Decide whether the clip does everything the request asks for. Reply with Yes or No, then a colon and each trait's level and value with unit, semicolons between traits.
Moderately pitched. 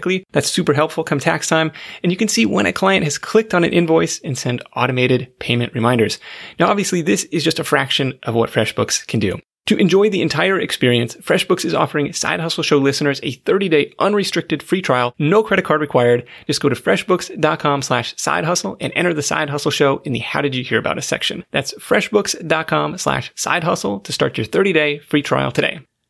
Yes: medium, 150 Hz